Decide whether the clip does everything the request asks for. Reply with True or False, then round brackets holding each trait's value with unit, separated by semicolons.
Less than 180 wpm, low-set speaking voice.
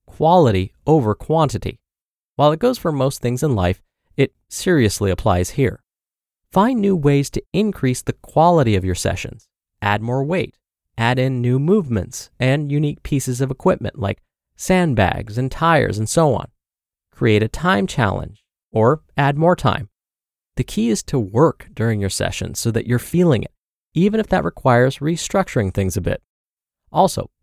True (160 wpm; 130 Hz)